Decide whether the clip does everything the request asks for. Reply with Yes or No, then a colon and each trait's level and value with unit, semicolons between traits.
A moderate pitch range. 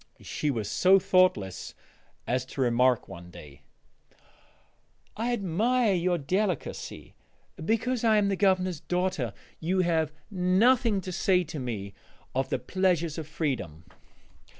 No: wide, 6.9 semitones